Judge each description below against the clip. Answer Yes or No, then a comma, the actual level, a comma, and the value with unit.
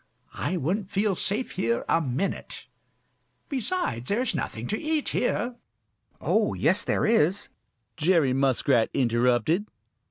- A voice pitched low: No, medium, 180 Hz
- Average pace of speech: No, slow, 125 wpm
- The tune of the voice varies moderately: No, wide, 8.7 semitones